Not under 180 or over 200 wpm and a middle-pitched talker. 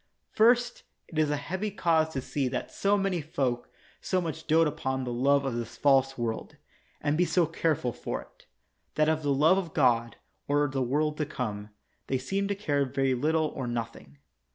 Yes: average, 195 wpm; medium, 145 Hz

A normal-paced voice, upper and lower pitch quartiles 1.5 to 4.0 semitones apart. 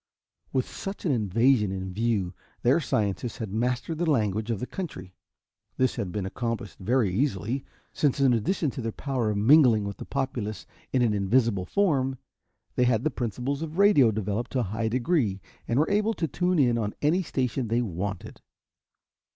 No: average, 180 wpm; average, 4.7 semitones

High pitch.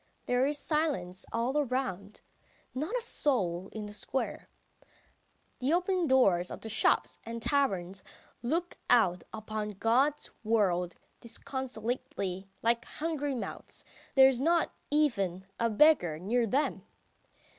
Yes: high, 235 Hz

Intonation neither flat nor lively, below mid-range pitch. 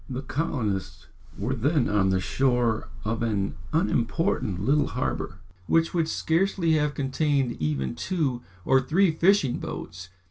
No: wide, 6.7 semitones; low, 130 Hz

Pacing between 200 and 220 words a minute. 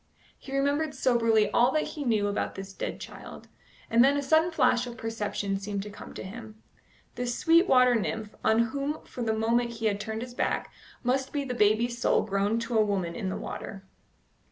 Yes: fast, 205 wpm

